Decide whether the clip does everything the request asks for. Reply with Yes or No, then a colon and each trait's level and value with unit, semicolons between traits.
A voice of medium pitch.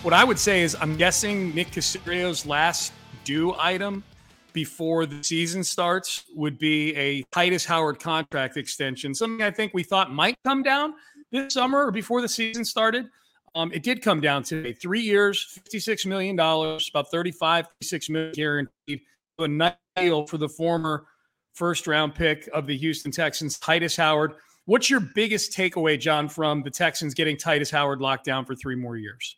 Yes: medium, 165 Hz